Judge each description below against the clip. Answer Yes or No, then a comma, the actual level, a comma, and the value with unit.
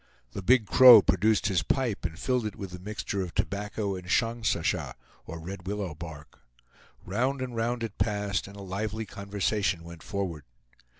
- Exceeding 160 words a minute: Yes, average, 170 wpm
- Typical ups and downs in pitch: Yes, average, 3.3 semitones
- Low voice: Yes, low, 100 Hz